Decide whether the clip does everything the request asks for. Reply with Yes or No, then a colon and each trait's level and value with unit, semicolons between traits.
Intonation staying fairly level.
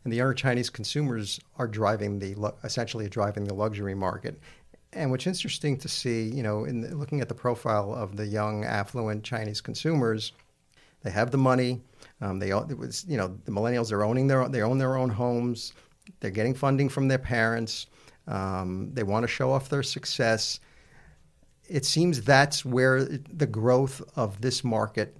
No: average, 4.0 semitones